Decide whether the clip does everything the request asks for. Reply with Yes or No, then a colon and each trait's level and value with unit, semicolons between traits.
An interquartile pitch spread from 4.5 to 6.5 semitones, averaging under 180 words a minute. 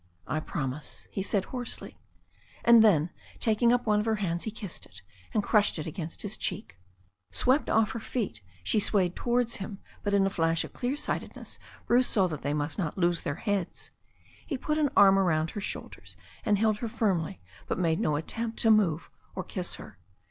No: wide, 5.4 semitones; average, 195 wpm